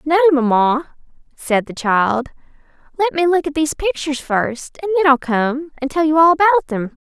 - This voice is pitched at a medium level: No, very high, 280 Hz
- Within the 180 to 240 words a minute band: Yes, average, 190 wpm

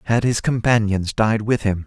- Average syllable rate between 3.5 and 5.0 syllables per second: Yes, 4.7 syllables/s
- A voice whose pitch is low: Yes, low, 110 Hz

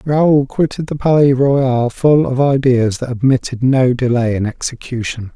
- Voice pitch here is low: Yes, low, 130 Hz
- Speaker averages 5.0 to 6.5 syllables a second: No, 4.4 syllables/s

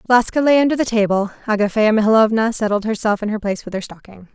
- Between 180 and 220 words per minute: Yes, fast, 205 wpm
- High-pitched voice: Yes, high, 215 Hz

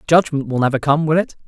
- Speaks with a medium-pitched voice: Yes, medium, 145 Hz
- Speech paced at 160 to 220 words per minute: No, fast, 245 wpm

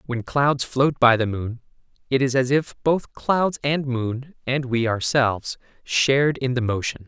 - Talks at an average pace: Yes, average, 180 wpm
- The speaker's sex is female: No, male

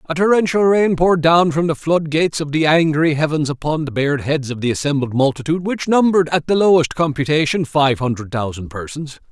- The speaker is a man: Yes, male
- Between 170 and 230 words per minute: Yes, average, 195 wpm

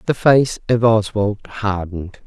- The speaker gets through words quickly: No, slow, 130 wpm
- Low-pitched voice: Yes, low, 105 Hz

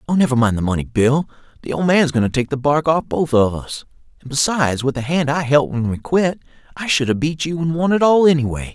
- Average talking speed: No, fast, 270 wpm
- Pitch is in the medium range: Yes, medium, 145 Hz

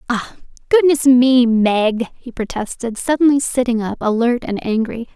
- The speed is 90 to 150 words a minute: Yes, average, 140 wpm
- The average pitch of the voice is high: Yes, high, 245 Hz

